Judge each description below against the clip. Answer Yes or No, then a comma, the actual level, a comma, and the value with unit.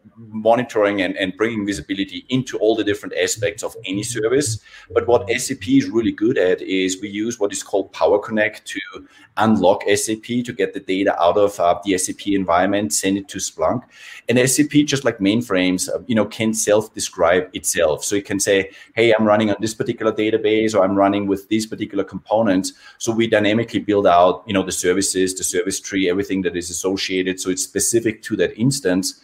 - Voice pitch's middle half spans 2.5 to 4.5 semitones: Yes, average, 3.2 semitones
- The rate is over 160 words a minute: Yes, average, 195 wpm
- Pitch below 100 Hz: No, low, 105 Hz